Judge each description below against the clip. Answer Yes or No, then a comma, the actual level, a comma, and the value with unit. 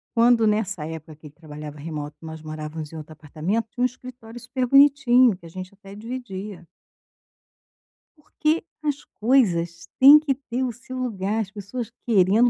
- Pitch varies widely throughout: Yes, wide, 7.4 semitones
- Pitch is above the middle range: Yes, high, 210 Hz